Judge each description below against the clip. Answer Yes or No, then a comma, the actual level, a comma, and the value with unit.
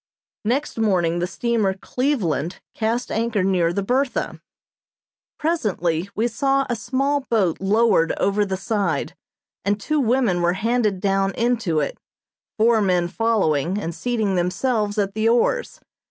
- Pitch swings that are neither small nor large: Yes, average, 4.3 semitones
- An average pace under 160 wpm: Yes, average, 140 wpm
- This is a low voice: No, high, 210 Hz